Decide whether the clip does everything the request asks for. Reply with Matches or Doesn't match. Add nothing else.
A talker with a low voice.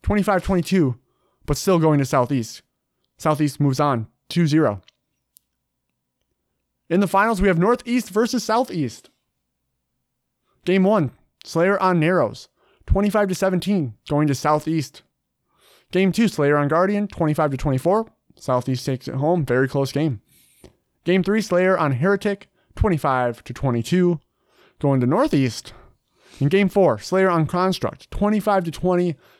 Doesn't match